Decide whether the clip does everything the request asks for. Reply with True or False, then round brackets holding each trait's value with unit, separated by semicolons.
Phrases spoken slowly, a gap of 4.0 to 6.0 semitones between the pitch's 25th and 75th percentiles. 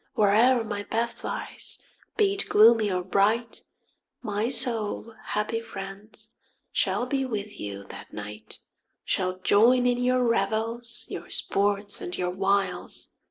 False (130 wpm; 3.2 semitones)